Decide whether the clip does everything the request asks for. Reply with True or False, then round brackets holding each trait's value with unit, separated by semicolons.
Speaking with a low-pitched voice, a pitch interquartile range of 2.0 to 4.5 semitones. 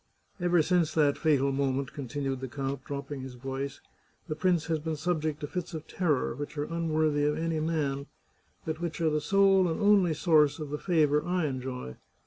False (150 Hz; 3.0 semitones)